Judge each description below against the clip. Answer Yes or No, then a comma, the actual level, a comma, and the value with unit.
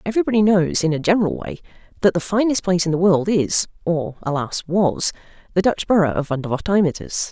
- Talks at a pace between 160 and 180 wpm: Yes, average, 165 wpm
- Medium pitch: Yes, medium, 180 Hz